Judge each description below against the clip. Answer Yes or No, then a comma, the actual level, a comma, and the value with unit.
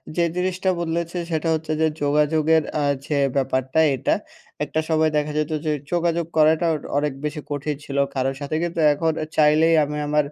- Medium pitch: Yes, medium, 155 Hz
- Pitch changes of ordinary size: No, narrow, 1.9 semitones